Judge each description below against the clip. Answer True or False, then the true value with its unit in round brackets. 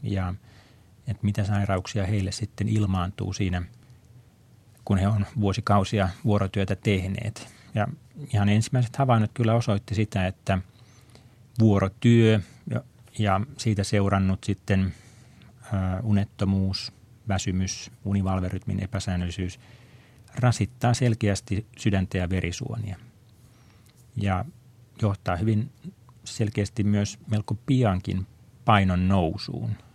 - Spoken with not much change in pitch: False (3.1 semitones)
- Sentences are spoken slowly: True (90 wpm)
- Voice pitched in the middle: False (105 Hz)